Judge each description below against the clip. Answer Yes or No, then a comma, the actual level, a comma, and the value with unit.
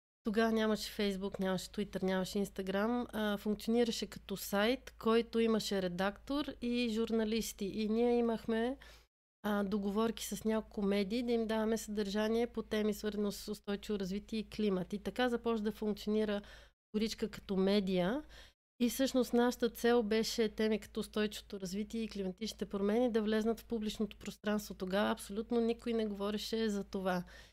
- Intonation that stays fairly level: Yes, narrow, 2.0 semitones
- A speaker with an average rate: Yes, average, 145 wpm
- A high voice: Yes, high, 215 Hz